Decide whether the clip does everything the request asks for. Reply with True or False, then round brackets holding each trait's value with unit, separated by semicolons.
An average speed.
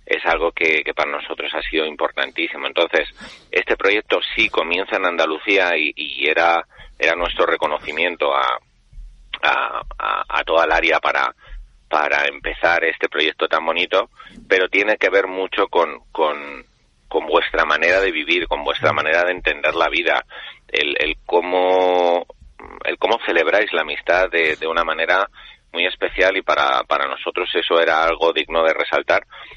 True (160 wpm)